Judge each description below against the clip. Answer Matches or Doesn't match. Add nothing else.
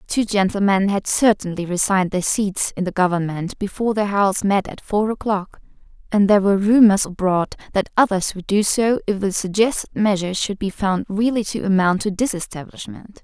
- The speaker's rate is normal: Matches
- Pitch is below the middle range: Doesn't match